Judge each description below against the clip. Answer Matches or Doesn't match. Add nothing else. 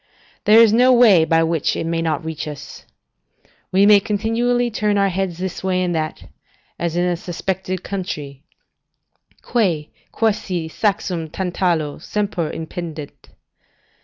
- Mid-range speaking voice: Matches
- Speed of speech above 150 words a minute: Doesn't match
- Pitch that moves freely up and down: Doesn't match